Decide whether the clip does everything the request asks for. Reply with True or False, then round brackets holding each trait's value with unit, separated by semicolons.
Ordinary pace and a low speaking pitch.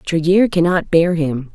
False (155 wpm; 170 Hz)